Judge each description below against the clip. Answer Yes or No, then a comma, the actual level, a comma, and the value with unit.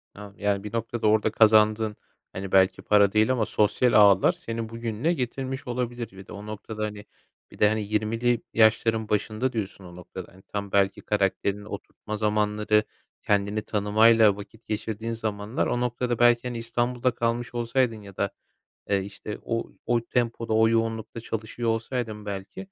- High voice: No, low, 110 Hz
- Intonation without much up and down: Yes, narrow, 2.1 semitones